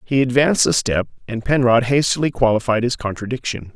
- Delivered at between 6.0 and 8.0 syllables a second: No, 5.8 syllables/s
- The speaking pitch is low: Yes, low, 125 Hz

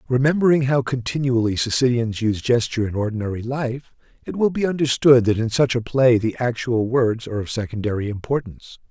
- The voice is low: Yes, low, 120 Hz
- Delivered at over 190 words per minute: No, average, 170 wpm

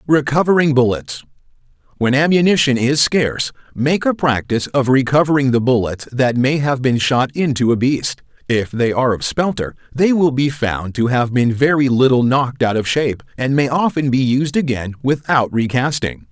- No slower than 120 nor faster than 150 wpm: No, average, 170 wpm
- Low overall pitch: Yes, low, 130 Hz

